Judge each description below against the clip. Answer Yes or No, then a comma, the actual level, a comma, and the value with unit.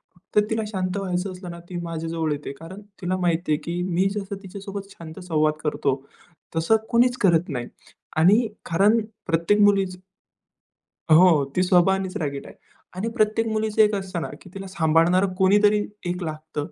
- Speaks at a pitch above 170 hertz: Yes, medium, 185 Hz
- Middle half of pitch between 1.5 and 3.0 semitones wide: No, average, 3.4 semitones